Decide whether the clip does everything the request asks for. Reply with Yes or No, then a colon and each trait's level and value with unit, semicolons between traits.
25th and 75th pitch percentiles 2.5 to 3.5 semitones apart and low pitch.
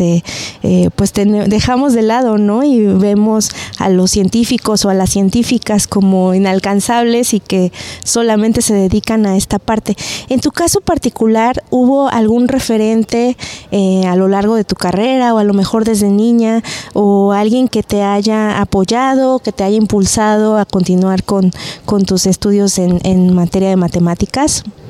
No: average, 3.1 semitones; high, 210 Hz